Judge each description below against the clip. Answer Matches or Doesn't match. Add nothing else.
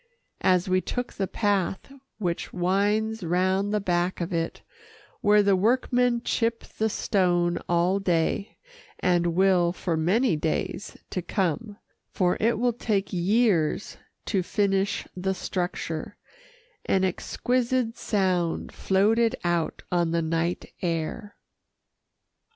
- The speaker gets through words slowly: Matches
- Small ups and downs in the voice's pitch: Doesn't match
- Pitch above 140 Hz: Matches